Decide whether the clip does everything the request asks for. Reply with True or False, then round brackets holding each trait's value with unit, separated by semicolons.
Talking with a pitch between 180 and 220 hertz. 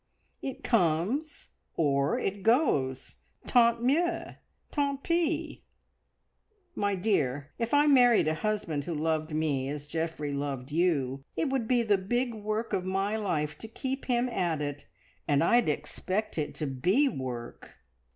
True (190 Hz)